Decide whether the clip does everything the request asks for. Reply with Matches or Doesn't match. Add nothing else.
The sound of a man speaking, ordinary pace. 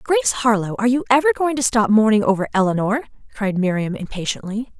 Doesn't match